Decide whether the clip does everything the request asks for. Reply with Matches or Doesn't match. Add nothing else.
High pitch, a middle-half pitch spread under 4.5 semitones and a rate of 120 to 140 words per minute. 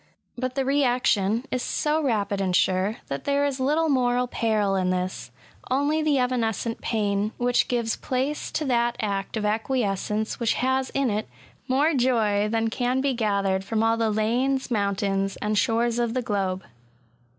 Doesn't match